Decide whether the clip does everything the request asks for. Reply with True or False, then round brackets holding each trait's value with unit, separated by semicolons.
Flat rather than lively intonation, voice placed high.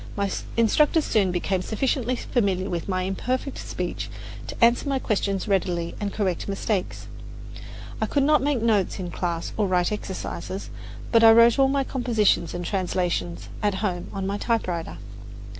False (4.3 semitones; 200 Hz)